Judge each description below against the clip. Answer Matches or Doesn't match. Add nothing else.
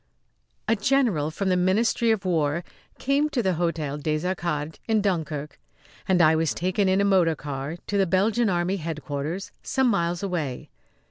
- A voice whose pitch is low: Doesn't match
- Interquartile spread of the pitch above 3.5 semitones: Matches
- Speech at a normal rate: Matches